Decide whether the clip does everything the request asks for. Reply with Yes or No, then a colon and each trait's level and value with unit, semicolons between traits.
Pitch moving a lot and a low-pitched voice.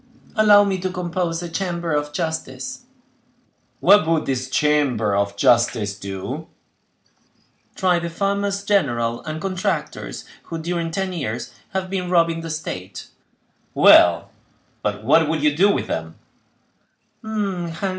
No: wide, 6.8 semitones; medium, 165 Hz